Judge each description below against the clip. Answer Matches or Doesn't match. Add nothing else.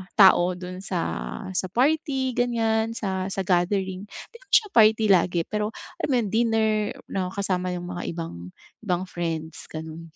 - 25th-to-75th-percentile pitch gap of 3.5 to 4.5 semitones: Matches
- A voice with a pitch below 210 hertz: Matches